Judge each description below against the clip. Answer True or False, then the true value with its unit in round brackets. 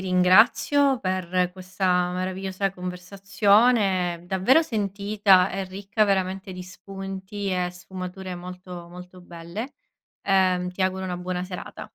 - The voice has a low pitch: False (185 Hz)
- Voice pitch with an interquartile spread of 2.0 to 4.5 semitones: False (1.5 semitones)